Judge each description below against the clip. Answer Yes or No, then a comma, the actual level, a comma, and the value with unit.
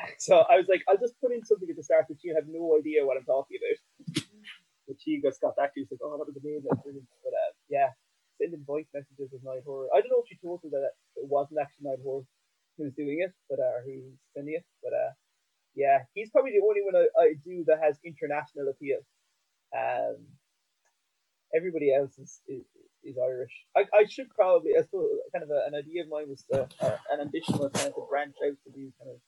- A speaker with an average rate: No, fast, 225 wpm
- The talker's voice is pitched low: No, medium, 160 Hz